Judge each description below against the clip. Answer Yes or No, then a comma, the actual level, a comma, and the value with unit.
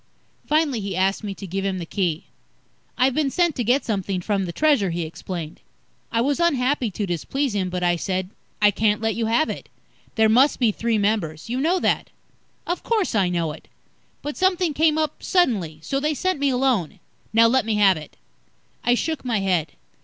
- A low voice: No, high, 220 Hz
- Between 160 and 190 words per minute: No, average, 200 wpm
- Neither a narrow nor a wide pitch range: No, wide, 6.8 semitones